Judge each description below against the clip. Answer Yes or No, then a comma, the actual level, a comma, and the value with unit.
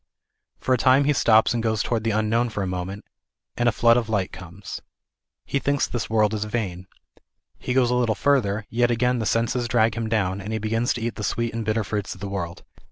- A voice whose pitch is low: Yes, low, 110 Hz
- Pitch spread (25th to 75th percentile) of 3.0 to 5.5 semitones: No, narrow, 2.6 semitones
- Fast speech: Yes, fast, 230 wpm